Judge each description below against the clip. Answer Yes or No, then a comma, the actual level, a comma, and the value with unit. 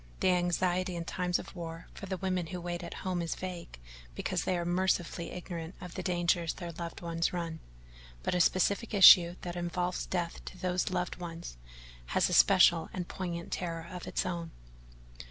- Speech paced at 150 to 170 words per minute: No, average, 185 wpm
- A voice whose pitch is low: No, medium, 175 Hz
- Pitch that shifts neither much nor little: No, narrow, 1.2 semitones